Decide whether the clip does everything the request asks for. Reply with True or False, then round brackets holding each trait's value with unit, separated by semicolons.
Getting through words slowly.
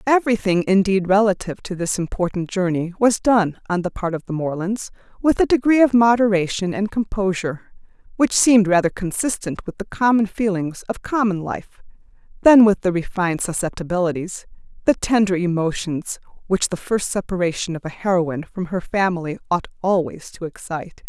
False (155 wpm)